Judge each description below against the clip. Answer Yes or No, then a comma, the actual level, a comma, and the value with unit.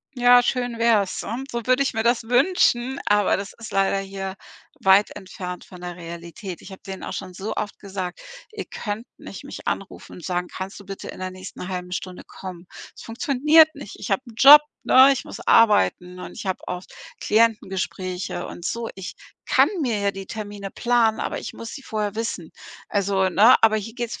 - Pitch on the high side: Yes, high, 205 Hz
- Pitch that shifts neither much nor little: Yes, average, 4.0 semitones